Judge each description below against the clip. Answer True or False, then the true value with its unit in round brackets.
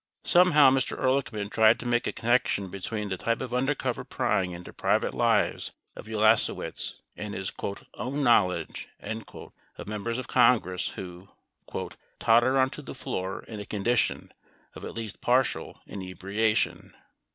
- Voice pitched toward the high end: False (110 Hz)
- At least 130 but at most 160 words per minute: True (140 wpm)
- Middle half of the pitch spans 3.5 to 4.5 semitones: True (4.2 semitones)